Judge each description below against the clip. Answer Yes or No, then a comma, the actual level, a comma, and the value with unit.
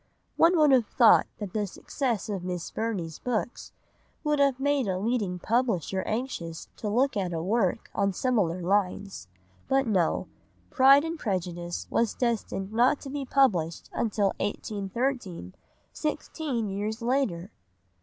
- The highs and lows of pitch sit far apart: Yes, wide, 5.8 semitones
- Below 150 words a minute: Yes, slow, 135 wpm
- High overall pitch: Yes, high, 215 Hz